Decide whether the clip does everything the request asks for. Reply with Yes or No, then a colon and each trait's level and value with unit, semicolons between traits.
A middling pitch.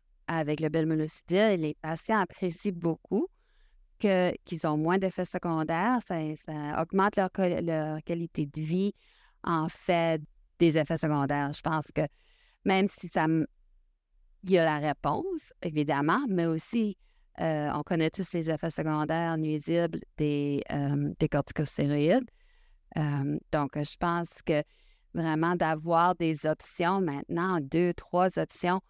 Yes: medium, 165 Hz